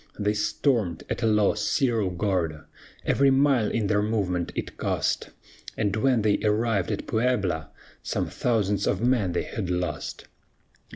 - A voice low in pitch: Yes, low, 105 Hz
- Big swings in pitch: No, average, 3.9 semitones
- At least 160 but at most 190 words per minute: No, average, 150 wpm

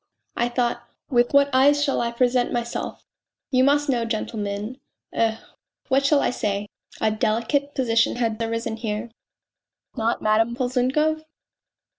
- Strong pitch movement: No, average, 2.9 semitones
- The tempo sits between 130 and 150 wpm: Yes, average, 140 wpm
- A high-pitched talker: Yes, high, 240 Hz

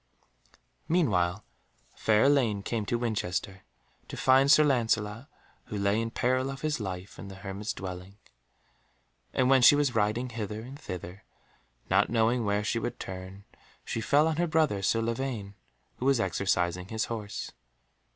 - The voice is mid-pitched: No, low, 110 Hz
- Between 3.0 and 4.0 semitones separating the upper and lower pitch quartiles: No, average, 4.5 semitones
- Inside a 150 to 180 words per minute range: Yes, average, 155 wpm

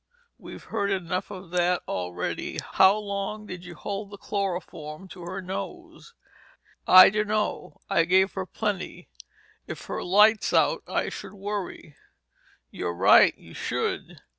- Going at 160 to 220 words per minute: No, average, 140 wpm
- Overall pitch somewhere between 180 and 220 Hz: Yes, high, 190 Hz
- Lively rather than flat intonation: No, narrow, 2.5 semitones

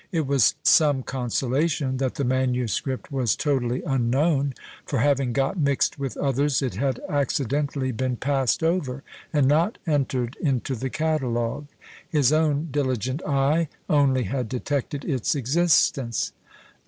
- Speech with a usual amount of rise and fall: No, narrow, 2.3 semitones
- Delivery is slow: Yes, slow, 130 wpm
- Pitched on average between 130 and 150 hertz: Yes, low, 135 Hz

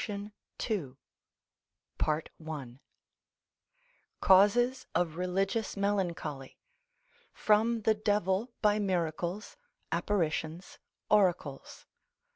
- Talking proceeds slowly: Yes, slow, 60 wpm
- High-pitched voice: Yes, high, 195 Hz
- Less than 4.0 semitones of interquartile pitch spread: No, average, 4.5 semitones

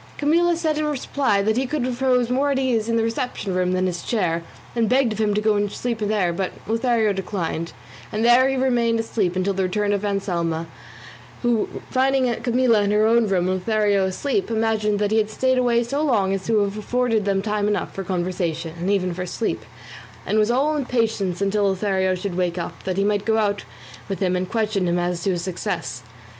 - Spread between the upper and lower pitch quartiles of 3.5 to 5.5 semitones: Yes, average, 4.0 semitones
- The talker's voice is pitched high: Yes, high, 210 Hz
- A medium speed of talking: No, fast, 220 wpm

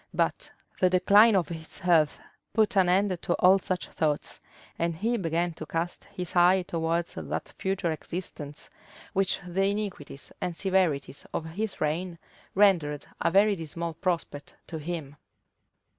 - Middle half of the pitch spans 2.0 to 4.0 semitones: Yes, average, 2.9 semitones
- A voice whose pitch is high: No, medium, 175 Hz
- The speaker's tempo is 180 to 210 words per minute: No, average, 145 wpm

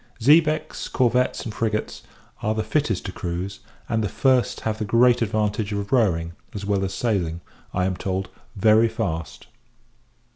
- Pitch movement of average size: Yes, average, 3.4 semitones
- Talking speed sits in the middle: Yes, average, 155 wpm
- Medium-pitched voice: No, low, 105 Hz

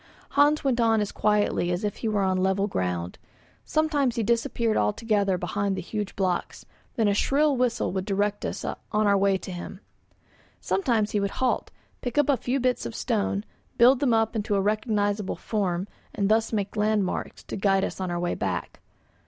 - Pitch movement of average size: Yes, average, 3.3 semitones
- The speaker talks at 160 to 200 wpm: Yes, average, 190 wpm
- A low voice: No, high, 210 Hz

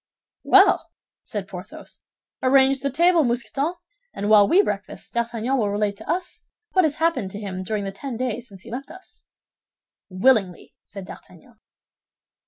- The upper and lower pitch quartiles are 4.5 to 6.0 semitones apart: Yes, average, 5.2 semitones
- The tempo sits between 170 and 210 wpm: No, average, 155 wpm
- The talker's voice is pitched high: Yes, high, 235 Hz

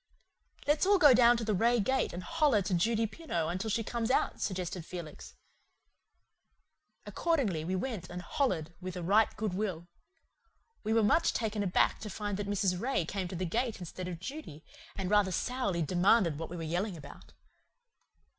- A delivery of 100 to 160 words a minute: No, average, 180 wpm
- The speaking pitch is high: Yes, high, 200 Hz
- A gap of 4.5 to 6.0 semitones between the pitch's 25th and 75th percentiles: Yes, average, 4.8 semitones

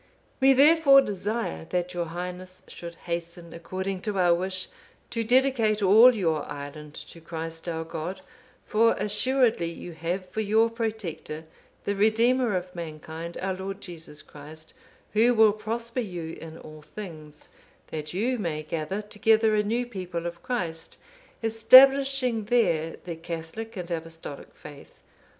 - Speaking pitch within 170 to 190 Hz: Yes, medium, 185 Hz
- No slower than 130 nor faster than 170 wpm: Yes, average, 140 wpm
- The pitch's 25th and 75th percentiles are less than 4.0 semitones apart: No, average, 5.2 semitones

